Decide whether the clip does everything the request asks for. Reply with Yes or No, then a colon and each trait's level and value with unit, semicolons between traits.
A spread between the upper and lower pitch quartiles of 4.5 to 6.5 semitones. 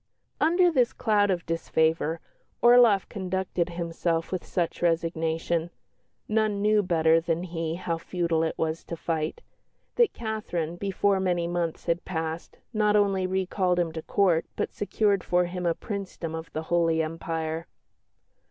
No: average, 3.2 semitones